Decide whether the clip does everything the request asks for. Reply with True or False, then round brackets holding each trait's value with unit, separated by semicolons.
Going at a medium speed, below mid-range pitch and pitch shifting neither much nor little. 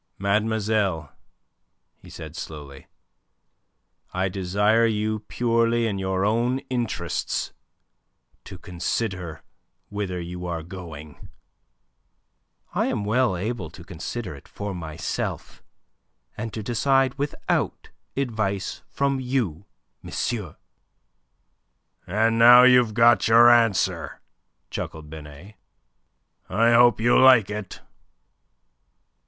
False (100 wpm; 105 Hz; 4.6 semitones)